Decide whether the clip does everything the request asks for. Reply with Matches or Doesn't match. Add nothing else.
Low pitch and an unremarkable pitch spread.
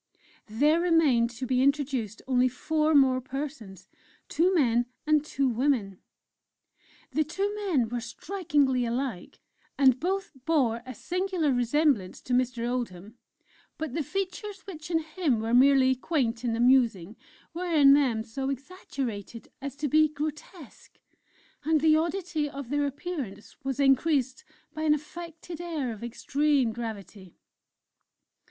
Doesn't match